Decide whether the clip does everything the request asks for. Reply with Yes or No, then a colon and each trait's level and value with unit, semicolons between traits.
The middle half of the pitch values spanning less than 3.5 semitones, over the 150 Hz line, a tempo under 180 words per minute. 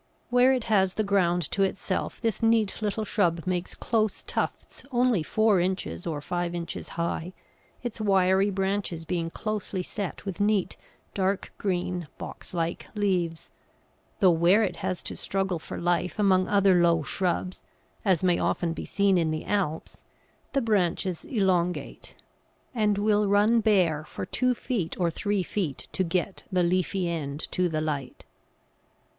Yes: average, 3.1 semitones; medium, 185 Hz; average, 155 wpm